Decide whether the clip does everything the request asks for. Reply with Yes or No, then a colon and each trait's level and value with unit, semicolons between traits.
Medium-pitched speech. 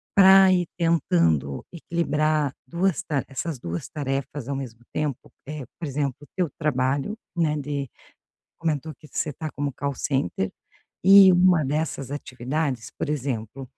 Yes: medium, 145 Hz